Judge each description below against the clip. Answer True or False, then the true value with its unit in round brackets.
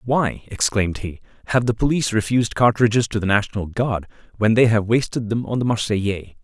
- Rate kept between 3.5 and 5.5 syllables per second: False (5.9 syllables/s)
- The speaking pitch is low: True (110 Hz)